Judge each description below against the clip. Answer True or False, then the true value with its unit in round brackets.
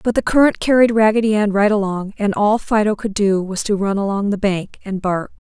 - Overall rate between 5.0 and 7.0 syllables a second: True (5.4 syllables/s)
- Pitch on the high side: True (205 Hz)